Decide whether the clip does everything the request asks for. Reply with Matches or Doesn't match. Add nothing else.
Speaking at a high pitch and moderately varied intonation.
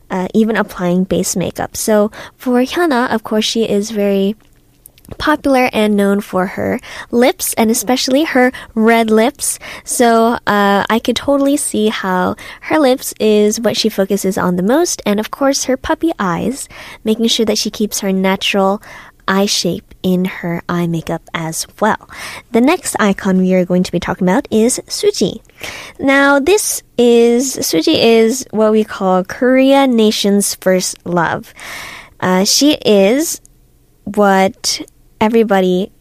Matches